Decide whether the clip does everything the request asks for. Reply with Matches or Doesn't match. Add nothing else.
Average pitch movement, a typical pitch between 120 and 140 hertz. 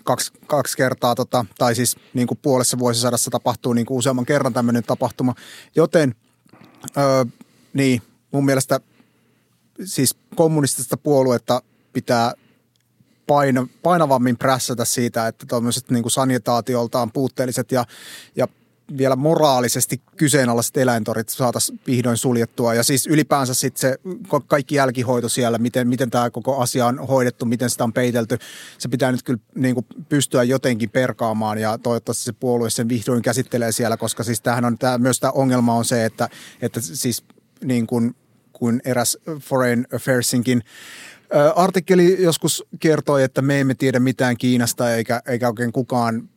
Doesn't match